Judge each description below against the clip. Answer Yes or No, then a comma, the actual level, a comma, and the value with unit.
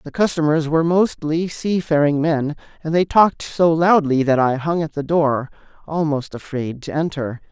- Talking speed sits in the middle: Yes, average, 170 wpm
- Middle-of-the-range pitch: Yes, medium, 155 Hz